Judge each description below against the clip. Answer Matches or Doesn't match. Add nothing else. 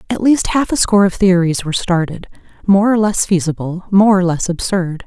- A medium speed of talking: Matches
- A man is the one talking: Doesn't match